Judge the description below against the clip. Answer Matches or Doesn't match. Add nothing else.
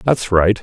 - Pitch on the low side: Matches